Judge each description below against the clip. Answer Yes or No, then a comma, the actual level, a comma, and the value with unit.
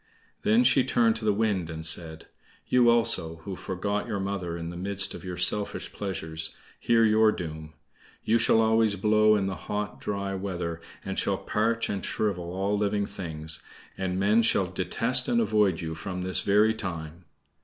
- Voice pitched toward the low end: Yes, low, 100 Hz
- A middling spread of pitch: Yes, average, 3.6 semitones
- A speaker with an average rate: Yes, average, 175 wpm